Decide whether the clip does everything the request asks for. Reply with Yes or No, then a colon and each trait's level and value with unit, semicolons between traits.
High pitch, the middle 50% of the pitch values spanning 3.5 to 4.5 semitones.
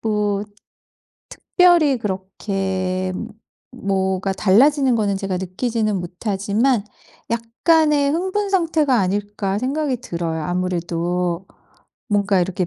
No: high, 200 Hz; wide, 5.6 semitones